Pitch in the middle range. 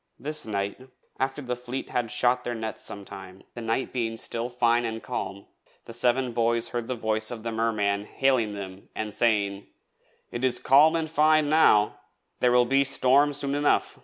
No: low, 120 Hz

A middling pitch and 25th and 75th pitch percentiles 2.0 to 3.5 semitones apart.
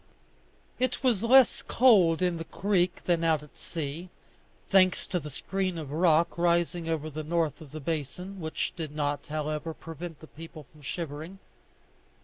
Yes: medium, 165 Hz; average, 2.8 semitones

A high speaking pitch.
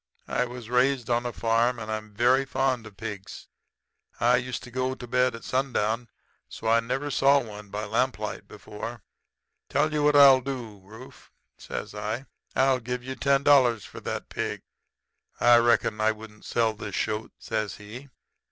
No: low, 120 Hz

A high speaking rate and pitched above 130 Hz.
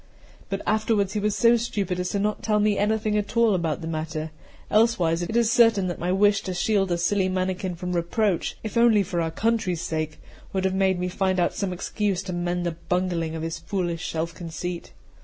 Yes: fast, 215 wpm; medium, 185 Hz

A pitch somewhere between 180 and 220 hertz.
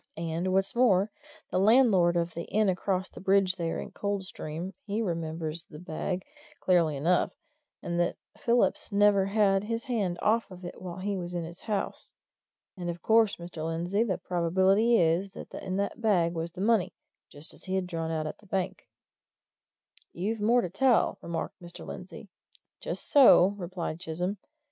Yes: medium, 185 Hz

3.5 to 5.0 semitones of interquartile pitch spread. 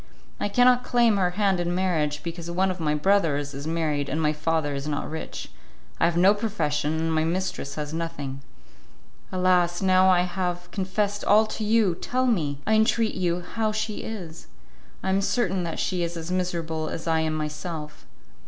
Yes: average, 3.8 semitones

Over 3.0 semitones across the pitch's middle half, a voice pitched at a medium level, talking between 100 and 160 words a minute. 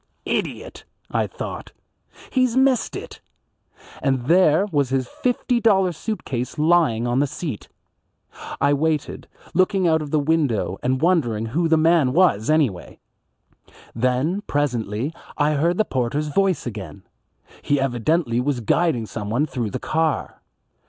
Yes: wide, 5.6 semitones; medium, 145 Hz; average, 140 wpm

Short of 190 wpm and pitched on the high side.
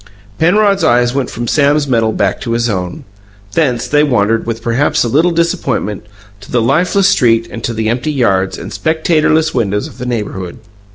No: average, 180 wpm; low, 120 Hz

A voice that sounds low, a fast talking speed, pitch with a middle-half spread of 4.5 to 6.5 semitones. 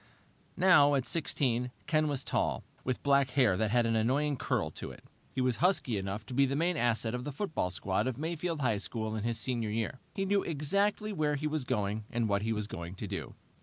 Yes: low, 130 Hz; fast, 225 wpm; average, 5.2 semitones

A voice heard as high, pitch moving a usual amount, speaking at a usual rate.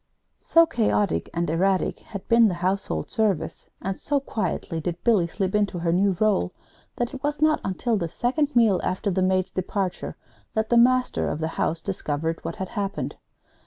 Yes: high, 195 Hz; average, 4.8 semitones; average, 180 wpm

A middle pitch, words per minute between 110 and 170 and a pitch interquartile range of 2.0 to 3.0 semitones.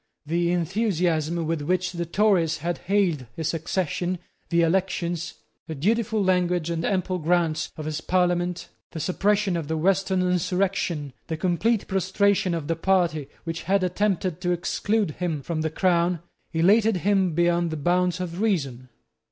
Yes: medium, 175 Hz; average, 150 wpm; narrow, 2.5 semitones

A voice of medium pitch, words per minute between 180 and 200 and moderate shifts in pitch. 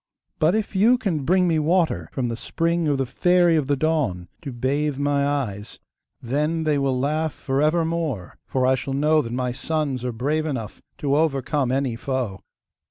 Yes: medium, 145 Hz; average, 185 wpm; average, 3.5 semitones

